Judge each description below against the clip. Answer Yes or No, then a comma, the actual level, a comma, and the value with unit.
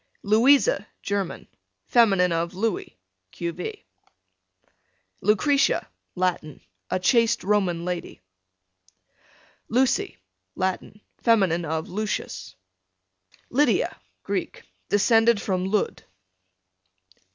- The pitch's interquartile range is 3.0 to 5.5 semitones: Yes, average, 4.3 semitones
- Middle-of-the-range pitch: No, high, 205 Hz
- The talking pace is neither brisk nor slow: No, slow, 75 wpm